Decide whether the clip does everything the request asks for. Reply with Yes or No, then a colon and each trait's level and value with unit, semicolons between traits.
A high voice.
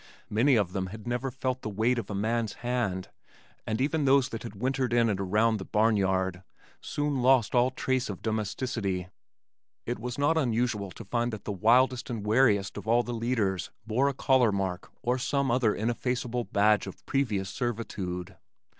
No: low, 115 Hz